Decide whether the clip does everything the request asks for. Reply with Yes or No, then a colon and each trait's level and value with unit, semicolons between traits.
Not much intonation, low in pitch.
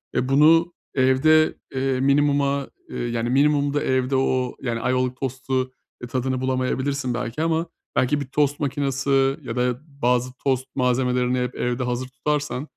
Yes: narrow, 1.9 semitones; low, 130 Hz